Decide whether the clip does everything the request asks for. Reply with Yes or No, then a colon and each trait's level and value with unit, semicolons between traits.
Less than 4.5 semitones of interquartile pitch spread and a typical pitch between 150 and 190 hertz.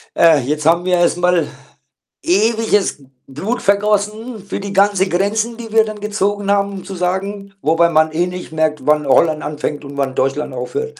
No: average, 4.8 semitones; medium, 185 Hz